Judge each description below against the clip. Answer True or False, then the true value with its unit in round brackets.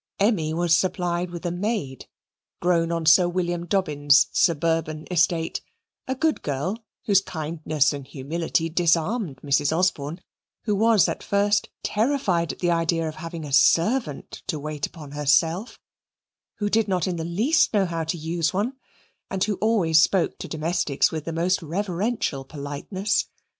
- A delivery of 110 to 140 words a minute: False (155 wpm)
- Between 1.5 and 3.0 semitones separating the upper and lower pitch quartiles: False (3.7 semitones)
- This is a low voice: False (170 Hz)